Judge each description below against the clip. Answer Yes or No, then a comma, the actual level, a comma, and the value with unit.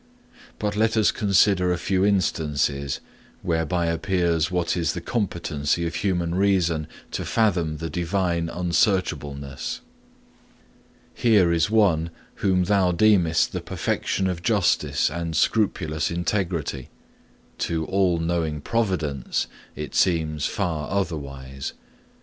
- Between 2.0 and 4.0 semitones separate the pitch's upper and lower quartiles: Yes, average, 3.4 semitones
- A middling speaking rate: No, slow, 115 wpm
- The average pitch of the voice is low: Yes, very low, 85 Hz